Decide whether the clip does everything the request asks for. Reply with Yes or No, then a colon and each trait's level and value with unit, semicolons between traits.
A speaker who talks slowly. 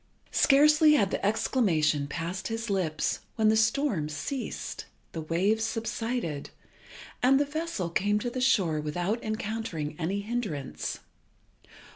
Yes: slow, 125 wpm